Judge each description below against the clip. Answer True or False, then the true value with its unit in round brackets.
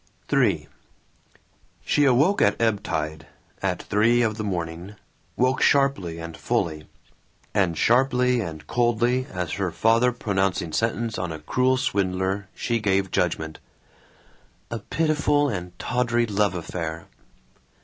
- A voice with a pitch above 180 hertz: False (105 Hz)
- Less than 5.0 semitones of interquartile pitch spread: False (5.6 semitones)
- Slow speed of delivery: True (125 wpm)